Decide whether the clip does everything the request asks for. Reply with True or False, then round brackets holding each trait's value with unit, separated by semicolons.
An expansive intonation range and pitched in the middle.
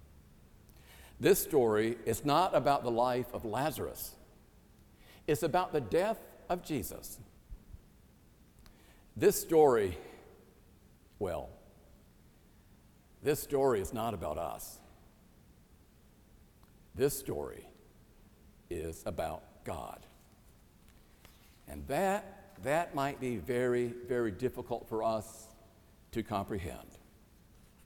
False (5.9 semitones; 115 Hz)